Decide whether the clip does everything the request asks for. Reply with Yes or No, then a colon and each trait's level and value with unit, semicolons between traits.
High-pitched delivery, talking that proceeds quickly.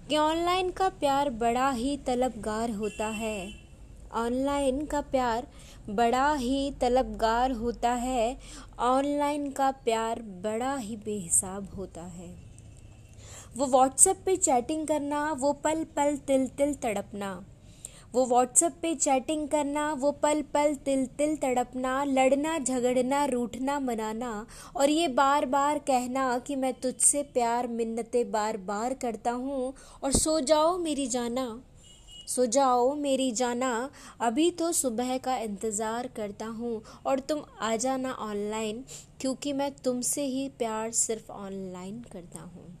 No: very high, 255 Hz; average, 135 wpm